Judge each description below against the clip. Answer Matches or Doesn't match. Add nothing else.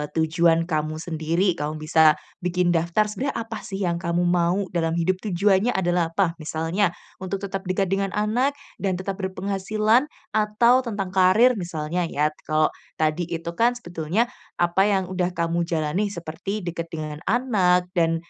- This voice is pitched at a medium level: Matches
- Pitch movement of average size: Matches